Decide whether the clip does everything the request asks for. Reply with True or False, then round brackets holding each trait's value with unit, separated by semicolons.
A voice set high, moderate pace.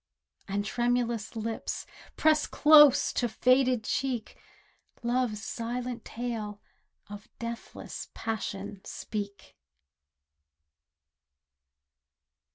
False (235 Hz; 70 wpm)